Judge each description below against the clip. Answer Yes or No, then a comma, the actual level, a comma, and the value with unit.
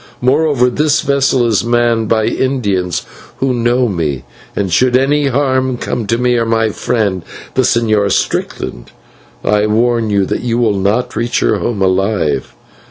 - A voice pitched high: No, low, 115 Hz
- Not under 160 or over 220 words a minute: Yes, average, 165 wpm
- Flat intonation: No, average, 3.5 semitones